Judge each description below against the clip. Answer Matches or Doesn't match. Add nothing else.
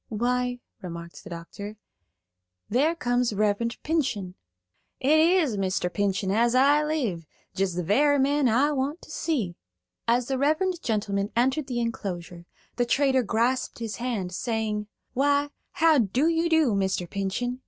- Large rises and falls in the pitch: Matches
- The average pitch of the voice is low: Doesn't match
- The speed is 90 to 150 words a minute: Matches